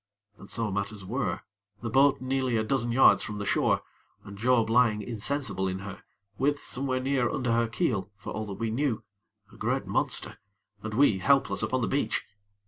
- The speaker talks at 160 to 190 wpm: Yes, average, 185 wpm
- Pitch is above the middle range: No, low, 115 Hz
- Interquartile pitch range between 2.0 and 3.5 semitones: No, average, 4.0 semitones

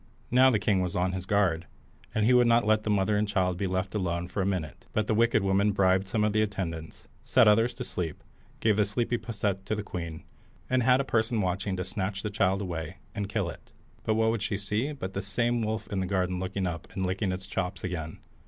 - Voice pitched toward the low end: Yes, low, 100 Hz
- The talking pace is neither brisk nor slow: No, fast, 235 wpm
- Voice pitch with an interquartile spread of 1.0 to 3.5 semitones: Yes, average, 2.8 semitones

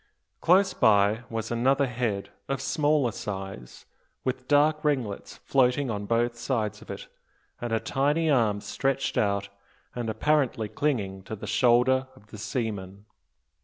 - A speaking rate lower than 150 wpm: Yes, average, 140 wpm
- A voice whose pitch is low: Yes, low, 120 Hz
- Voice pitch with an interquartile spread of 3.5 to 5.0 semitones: Yes, average, 4.6 semitones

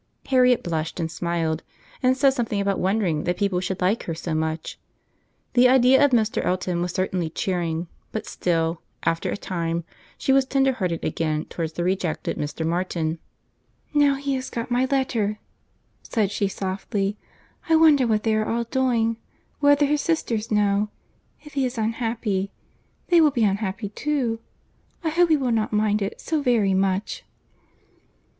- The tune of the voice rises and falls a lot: Yes, wide, 6.2 semitones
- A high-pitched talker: Yes, high, 210 Hz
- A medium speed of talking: Yes, average, 160 wpm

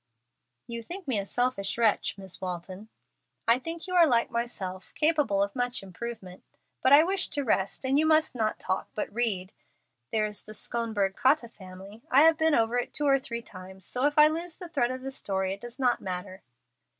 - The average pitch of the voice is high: Yes, high, 235 Hz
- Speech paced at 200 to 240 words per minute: Yes, fast, 205 wpm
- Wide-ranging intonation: Yes, wide, 6.2 semitones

